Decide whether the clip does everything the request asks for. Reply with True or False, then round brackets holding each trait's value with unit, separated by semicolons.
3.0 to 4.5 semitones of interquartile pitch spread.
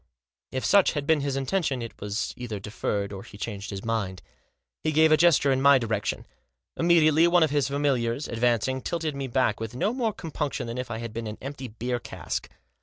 False (4.9 semitones)